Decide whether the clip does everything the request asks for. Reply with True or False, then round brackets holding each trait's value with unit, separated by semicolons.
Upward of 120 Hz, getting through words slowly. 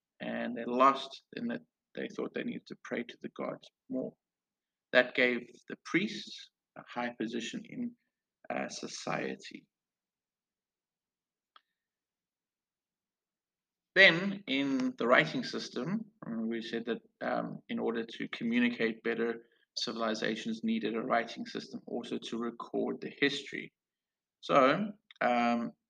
True (135 Hz; 120 wpm)